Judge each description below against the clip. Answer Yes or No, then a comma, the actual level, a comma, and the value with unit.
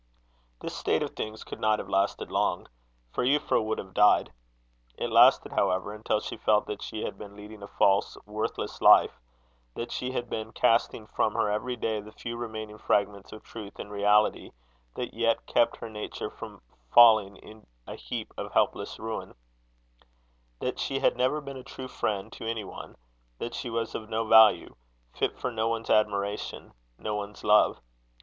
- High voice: No, low, 110 Hz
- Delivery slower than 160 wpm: No, average, 180 wpm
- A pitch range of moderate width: No, narrow, 1.8 semitones